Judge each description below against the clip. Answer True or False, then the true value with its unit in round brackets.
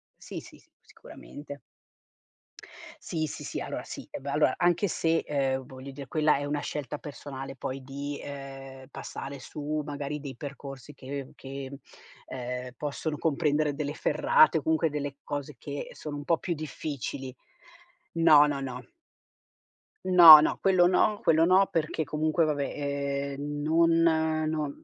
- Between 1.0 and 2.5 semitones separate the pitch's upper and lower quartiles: True (2.2 semitones)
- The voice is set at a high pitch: False (145 Hz)